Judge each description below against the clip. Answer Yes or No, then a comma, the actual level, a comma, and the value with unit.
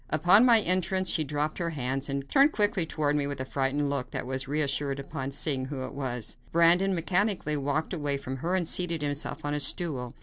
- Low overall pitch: No, medium, 145 Hz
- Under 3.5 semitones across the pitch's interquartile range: No, average, 4.0 semitones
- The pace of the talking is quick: Yes, fast, 210 wpm